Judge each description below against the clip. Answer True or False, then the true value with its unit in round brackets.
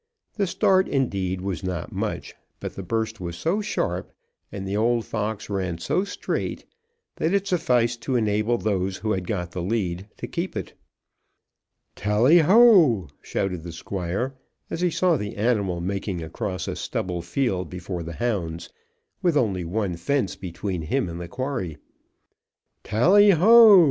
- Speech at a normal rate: True (155 wpm)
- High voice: False (105 Hz)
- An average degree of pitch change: False (6.7 semitones)